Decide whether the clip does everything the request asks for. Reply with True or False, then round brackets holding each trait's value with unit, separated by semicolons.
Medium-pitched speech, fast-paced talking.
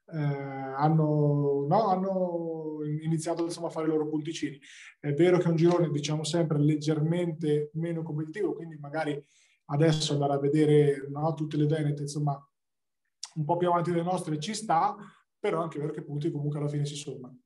True (155 Hz; 180 wpm)